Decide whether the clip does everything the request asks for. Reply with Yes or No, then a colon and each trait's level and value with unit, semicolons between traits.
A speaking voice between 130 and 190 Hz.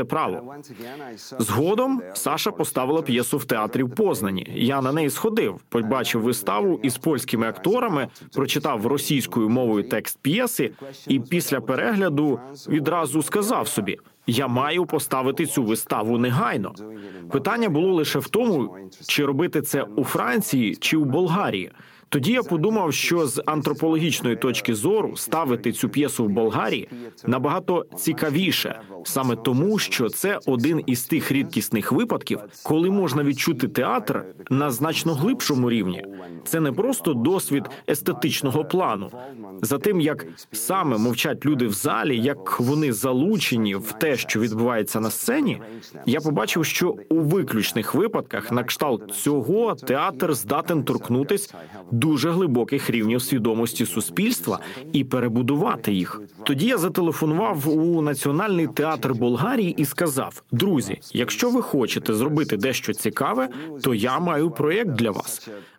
Yes: medium, 140 Hz